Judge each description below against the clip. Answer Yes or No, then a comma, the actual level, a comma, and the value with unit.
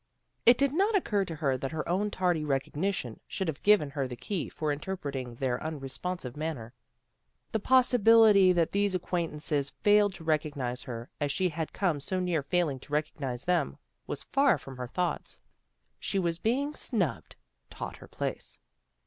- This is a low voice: No, medium, 165 Hz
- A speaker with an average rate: Yes, average, 165 wpm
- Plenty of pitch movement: Yes, wide, 5.8 semitones